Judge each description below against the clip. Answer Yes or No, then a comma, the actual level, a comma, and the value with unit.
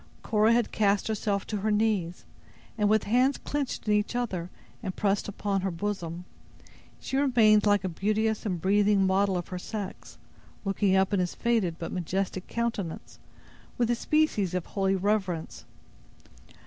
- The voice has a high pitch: Yes, high, 205 Hz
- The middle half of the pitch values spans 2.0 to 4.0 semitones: Yes, narrow, 2.5 semitones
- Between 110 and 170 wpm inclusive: Yes, average, 160 wpm